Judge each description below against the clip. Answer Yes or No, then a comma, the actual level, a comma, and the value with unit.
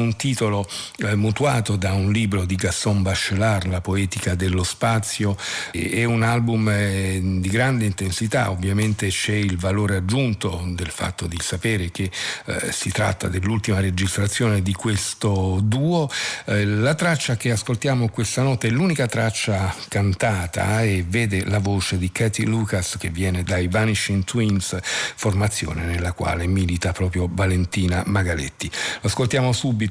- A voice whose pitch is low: Yes, low, 100 Hz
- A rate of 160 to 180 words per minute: No, average, 135 wpm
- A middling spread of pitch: Yes, average, 3.1 semitones